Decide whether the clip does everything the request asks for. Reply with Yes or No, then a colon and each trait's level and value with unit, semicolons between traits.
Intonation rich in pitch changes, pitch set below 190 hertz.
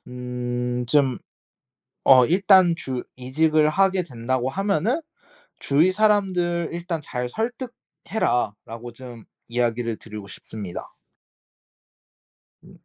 Yes: wide, 7.0 semitones; low, 135 Hz